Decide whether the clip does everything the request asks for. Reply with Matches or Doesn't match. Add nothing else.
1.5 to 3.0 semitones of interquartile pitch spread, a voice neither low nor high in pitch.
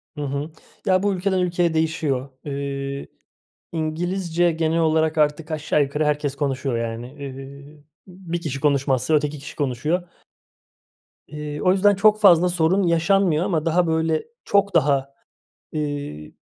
Doesn't match